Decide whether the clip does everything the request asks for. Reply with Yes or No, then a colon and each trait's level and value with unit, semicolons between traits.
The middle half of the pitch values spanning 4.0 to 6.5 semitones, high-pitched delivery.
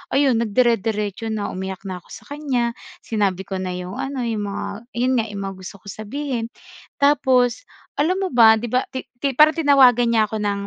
Yes: average, 4.5 semitones; high, 230 Hz